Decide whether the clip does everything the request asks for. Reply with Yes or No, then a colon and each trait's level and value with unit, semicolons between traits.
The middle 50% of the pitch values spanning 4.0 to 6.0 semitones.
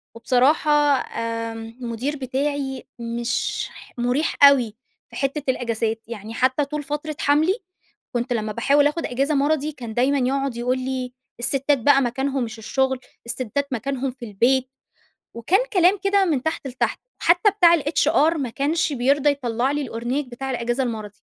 No: average, 3.4 semitones